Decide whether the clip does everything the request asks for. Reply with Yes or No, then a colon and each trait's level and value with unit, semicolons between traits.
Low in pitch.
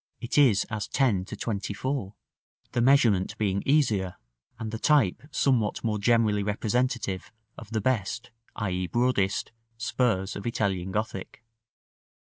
Yes: low, 110 Hz